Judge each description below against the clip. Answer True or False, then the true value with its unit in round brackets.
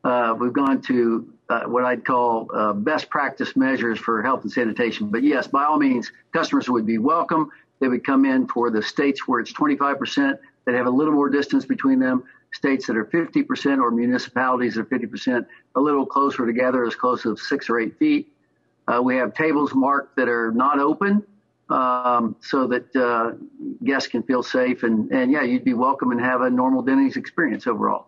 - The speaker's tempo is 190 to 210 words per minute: True (200 wpm)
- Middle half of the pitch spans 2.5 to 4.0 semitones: False (4.4 semitones)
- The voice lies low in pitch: True (130 Hz)